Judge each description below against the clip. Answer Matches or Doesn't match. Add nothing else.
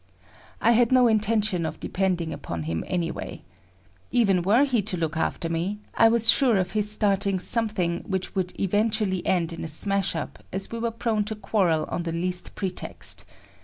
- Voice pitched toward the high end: Matches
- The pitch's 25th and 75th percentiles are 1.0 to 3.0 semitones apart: Doesn't match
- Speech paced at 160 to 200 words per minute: Matches